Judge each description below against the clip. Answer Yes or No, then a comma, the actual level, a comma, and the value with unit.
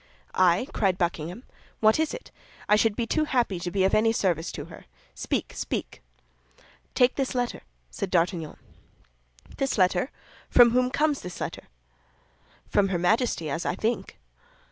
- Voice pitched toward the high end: Yes, high, 205 Hz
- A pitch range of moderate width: No, wide, 5.7 semitones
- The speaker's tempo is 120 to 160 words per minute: Yes, average, 155 wpm